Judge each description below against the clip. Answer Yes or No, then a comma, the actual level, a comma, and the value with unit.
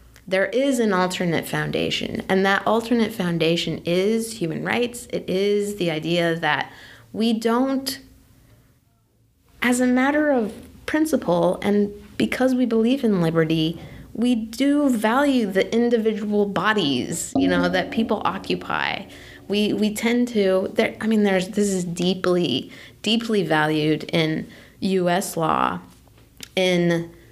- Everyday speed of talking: No, slow, 125 wpm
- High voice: Yes, high, 195 Hz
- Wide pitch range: Yes, wide, 5.7 semitones